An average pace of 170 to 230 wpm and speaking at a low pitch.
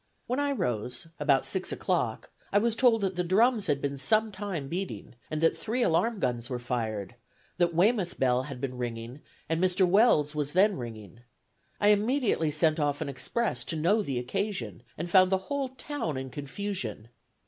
No: average, 180 wpm; medium, 165 Hz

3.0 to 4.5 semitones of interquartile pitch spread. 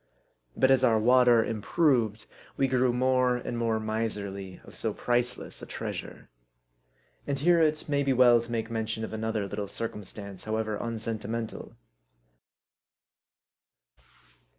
No: narrow, 2.6 semitones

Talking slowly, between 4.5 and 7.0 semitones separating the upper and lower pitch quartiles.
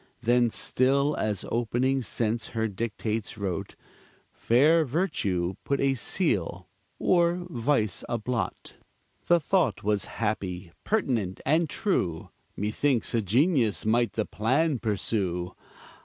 Yes: slow, 115 wpm; average, 5.2 semitones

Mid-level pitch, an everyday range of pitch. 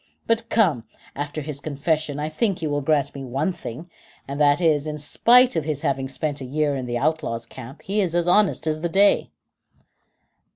Yes: medium, 150 Hz; average, 3.5 semitones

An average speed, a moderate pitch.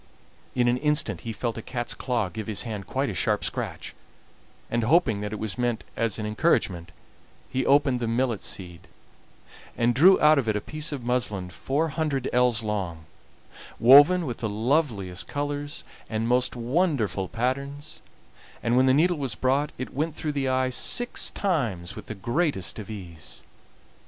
No: average, 170 wpm; low, 120 Hz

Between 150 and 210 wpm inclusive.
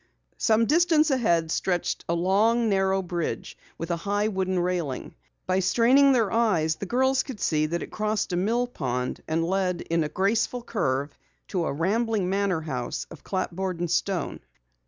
Yes: average, 170 wpm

